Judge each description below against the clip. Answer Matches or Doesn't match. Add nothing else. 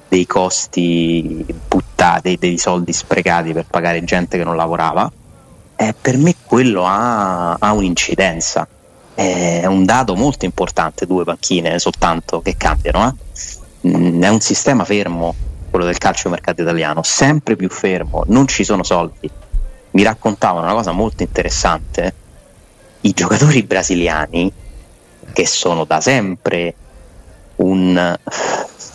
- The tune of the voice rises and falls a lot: Doesn't match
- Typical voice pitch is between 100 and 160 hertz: Doesn't match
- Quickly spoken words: Doesn't match